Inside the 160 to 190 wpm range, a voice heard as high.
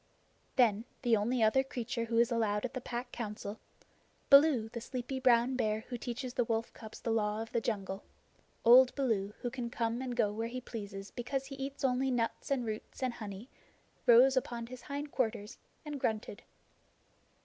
Yes: average, 180 wpm; high, 235 Hz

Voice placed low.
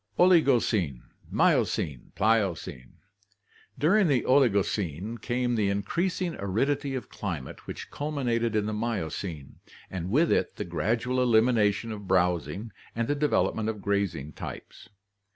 Yes: low, 110 Hz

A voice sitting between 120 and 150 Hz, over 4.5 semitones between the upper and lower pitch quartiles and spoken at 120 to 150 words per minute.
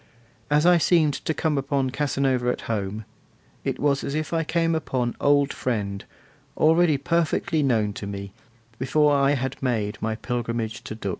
No: low, 135 Hz; average, 5.0 semitones; average, 165 wpm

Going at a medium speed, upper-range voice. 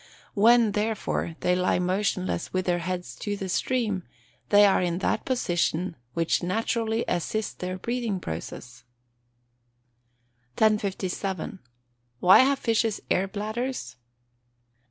No: slow, 115 wpm; high, 195 Hz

